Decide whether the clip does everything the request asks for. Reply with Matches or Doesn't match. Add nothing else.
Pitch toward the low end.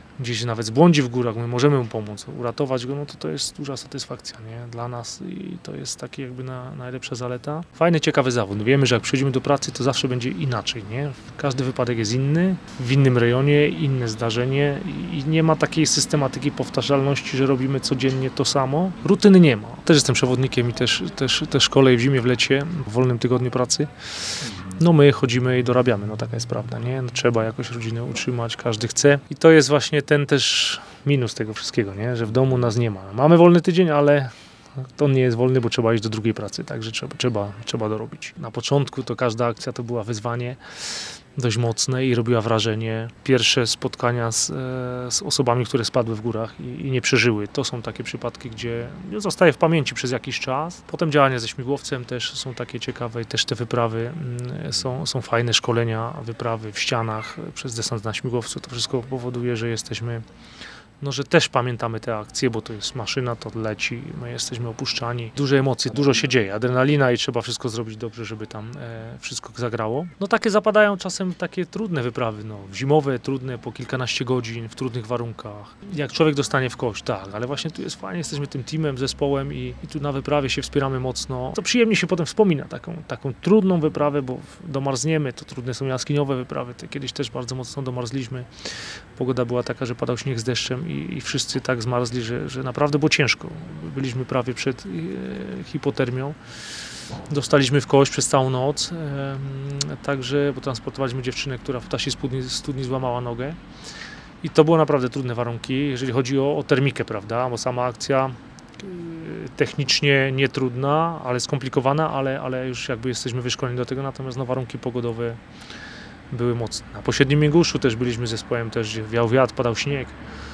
Matches